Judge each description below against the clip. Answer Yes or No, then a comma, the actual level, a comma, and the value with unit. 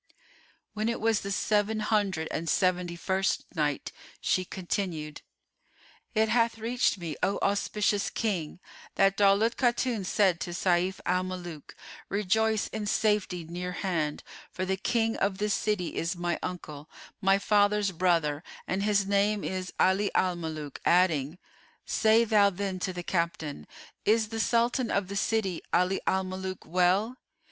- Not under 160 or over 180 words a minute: No, average, 150 wpm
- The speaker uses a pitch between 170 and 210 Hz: Yes, high, 190 Hz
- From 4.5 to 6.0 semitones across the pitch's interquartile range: No, average, 3.0 semitones